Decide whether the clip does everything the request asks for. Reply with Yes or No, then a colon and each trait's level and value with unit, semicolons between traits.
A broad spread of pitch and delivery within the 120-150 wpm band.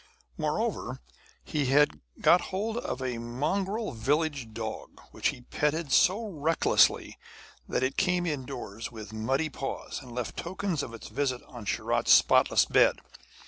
Yes: wide, 5.8 semitones; average, 140 wpm